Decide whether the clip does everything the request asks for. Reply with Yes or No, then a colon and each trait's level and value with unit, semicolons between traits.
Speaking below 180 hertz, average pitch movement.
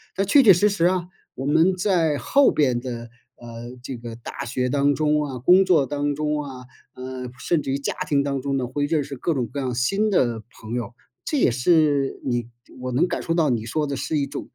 Yes: medium, 140 Hz; average, 4.2 semitones